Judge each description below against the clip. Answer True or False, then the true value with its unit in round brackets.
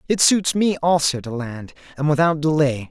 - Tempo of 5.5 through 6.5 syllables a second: False (4.8 syllables/s)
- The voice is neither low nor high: True (150 Hz)